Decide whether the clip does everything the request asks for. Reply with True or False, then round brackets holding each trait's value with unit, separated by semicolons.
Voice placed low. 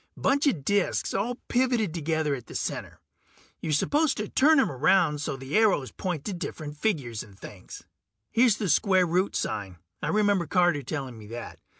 False (170 Hz)